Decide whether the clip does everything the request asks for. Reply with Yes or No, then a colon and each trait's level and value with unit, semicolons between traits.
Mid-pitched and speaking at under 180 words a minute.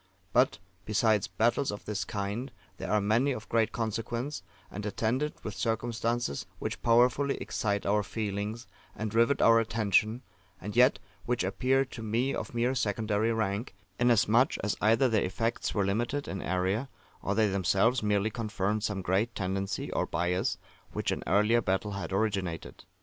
No: low, 110 Hz; average, 155 wpm